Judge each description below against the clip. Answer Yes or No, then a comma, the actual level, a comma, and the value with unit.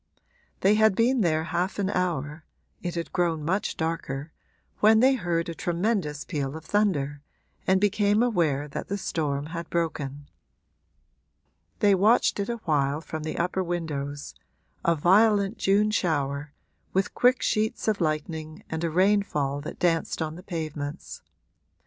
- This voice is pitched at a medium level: Yes, medium, 170 Hz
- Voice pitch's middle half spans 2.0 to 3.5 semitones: No, average, 4.8 semitones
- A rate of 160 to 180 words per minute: No, average, 150 wpm